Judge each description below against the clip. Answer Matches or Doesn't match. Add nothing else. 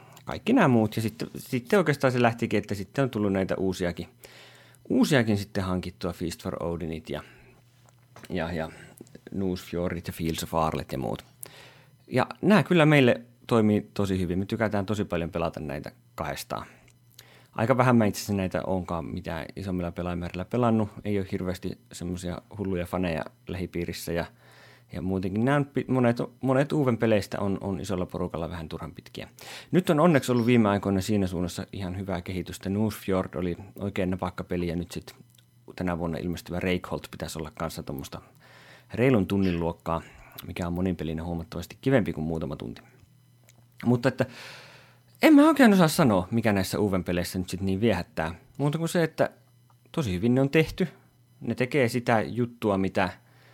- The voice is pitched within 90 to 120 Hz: Matches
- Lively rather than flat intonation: Matches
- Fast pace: Matches